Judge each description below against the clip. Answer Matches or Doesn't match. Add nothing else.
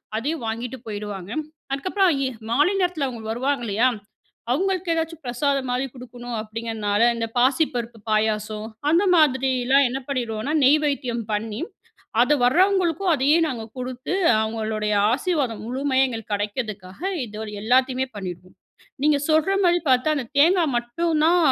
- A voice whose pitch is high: Matches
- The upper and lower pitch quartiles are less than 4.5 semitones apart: Doesn't match